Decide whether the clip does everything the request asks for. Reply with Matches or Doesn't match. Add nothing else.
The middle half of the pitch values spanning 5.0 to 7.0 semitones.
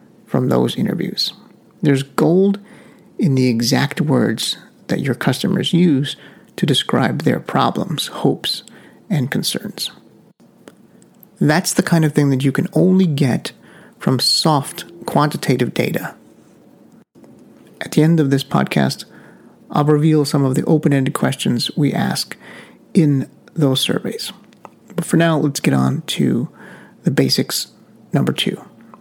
Doesn't match